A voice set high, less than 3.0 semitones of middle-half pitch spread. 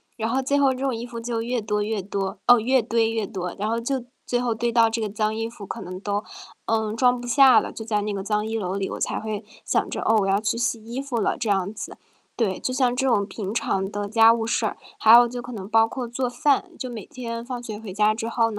Yes: high, 225 Hz; narrow, 2.5 semitones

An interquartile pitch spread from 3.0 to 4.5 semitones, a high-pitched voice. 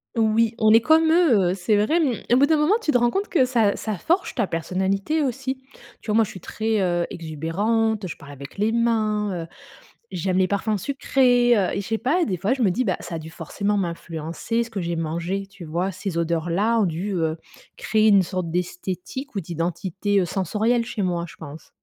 No: average, 4.9 semitones; high, 200 Hz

